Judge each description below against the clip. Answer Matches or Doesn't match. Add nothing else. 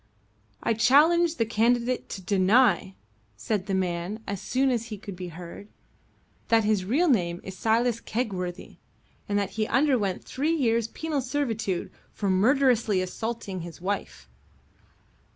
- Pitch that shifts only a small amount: Doesn't match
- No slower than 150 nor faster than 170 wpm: Doesn't match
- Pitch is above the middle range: Matches